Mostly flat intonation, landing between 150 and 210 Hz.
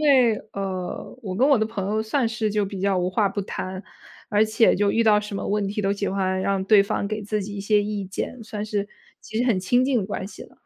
Yes: narrow, 1.9 semitones; high, 205 Hz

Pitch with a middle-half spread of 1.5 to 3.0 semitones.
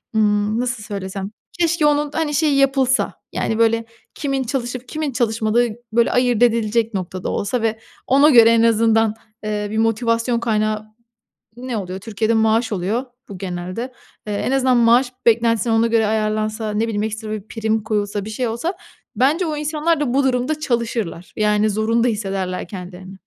Yes: average, 2.7 semitones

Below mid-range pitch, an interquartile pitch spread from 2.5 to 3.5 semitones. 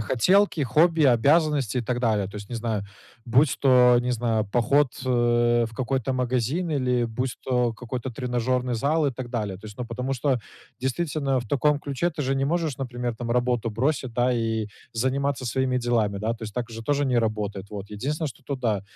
Yes: low, 125 Hz; average, 2.9 semitones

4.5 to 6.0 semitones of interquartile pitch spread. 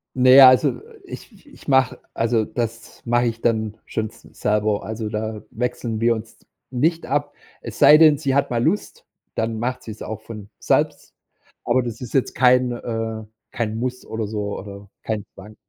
No: narrow, 2.6 semitones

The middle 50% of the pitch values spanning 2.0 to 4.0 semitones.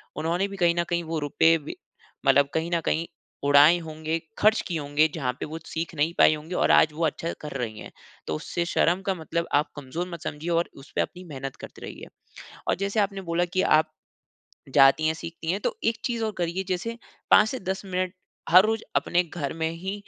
Yes: average, 3.1 semitones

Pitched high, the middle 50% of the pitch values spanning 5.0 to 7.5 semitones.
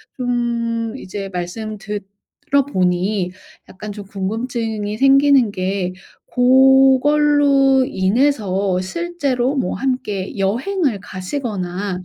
Yes: high, 225 Hz; wide, 5.5 semitones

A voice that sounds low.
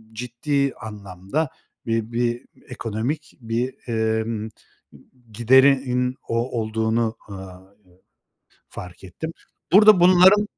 Yes: low, 120 Hz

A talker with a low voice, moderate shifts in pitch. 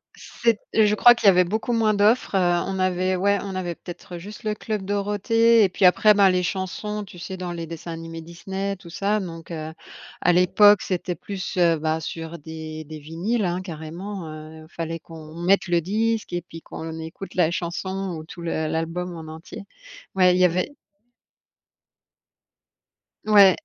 No: medium, 180 Hz; average, 3.3 semitones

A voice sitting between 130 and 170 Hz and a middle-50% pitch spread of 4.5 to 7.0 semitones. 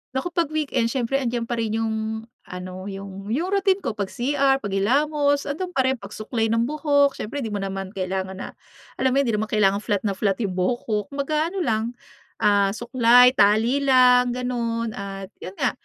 No: high, 230 Hz; average, 5.2 semitones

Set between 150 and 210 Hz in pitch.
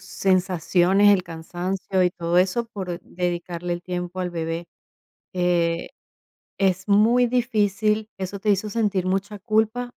Yes: medium, 185 Hz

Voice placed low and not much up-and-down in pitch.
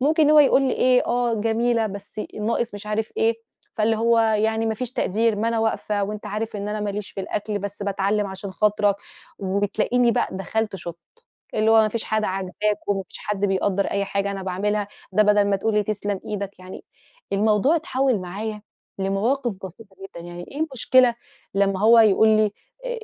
No: high, 210 Hz; narrow, 2.2 semitones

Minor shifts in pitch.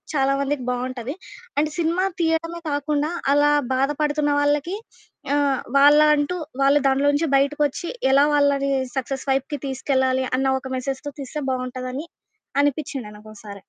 Yes: narrow, 1.8 semitones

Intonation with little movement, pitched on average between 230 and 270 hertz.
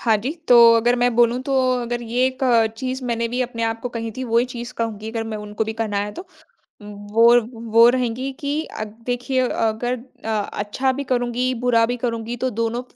Yes: narrow, 1.7 semitones; high, 235 Hz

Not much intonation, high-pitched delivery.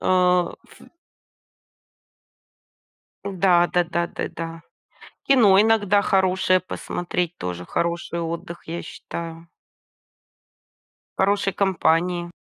No: narrow, 2.1 semitones; medium, 175 Hz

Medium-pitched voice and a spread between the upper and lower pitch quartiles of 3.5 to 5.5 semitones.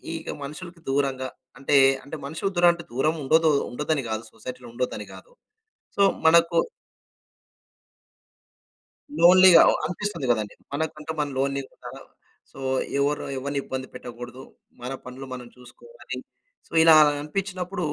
Yes: medium, 145 Hz; average, 4.3 semitones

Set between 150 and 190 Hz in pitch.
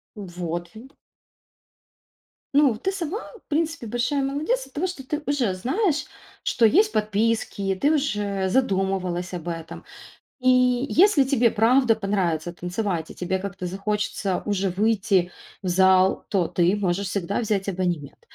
No: high, 205 Hz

